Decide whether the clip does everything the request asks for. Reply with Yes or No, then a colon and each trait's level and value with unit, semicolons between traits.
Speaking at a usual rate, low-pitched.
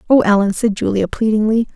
No: average, 170 wpm; high, 215 Hz